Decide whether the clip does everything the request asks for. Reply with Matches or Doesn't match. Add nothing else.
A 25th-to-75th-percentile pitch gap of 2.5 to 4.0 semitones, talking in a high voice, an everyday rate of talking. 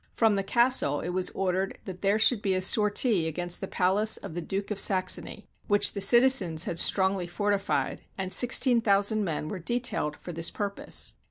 Matches